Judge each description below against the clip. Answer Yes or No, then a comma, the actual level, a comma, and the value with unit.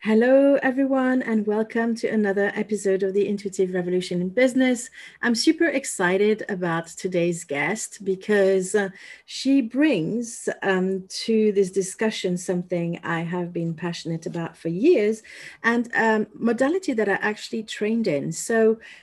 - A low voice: No, high, 210 Hz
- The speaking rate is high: No, slow, 135 wpm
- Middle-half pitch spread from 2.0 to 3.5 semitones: No, average, 3.9 semitones